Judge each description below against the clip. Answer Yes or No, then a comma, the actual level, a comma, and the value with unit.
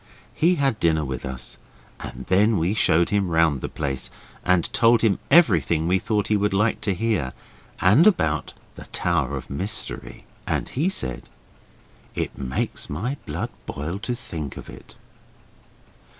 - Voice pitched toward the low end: Yes, very low, 95 Hz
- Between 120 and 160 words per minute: Yes, average, 155 wpm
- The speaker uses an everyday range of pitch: No, wide, 6.4 semitones